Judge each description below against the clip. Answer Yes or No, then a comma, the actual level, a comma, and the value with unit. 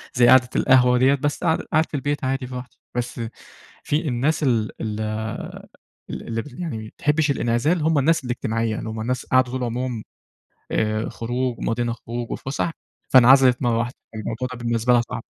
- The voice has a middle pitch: No, low, 125 Hz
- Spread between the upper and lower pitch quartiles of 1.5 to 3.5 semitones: Yes, average, 2.7 semitones